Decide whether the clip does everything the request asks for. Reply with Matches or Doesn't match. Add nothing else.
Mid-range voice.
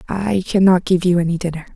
Matches